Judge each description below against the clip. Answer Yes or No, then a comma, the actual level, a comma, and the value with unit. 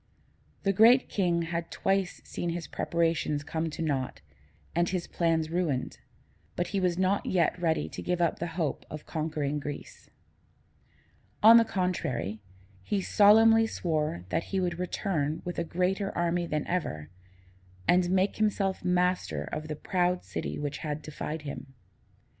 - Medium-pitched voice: Yes, medium, 170 Hz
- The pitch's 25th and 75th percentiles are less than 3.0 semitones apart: No, average, 3.3 semitones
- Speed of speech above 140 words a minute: Yes, average, 155 wpm